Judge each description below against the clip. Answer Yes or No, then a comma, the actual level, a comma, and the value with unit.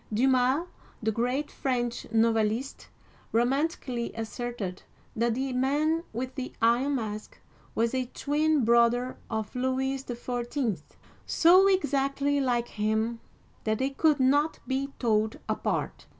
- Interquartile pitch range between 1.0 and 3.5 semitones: Yes, average, 3.1 semitones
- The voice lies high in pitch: Yes, very high, 250 Hz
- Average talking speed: No, slow, 125 wpm